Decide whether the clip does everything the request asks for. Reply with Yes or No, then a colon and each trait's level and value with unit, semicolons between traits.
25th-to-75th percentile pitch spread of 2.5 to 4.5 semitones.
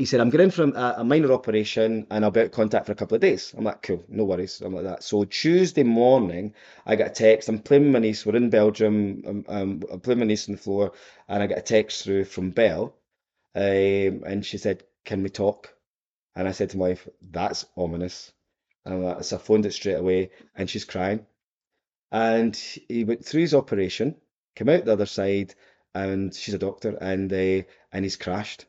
Yes: average, 2.8 semitones